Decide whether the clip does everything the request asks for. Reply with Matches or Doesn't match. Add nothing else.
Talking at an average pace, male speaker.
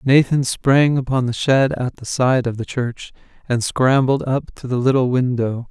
Matches